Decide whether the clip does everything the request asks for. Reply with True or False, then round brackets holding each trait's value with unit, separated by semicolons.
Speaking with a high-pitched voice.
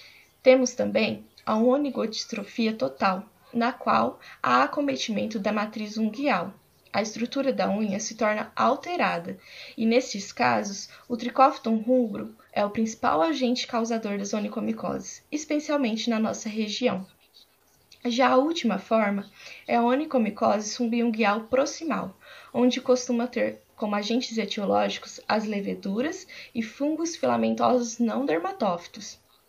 True (230 Hz)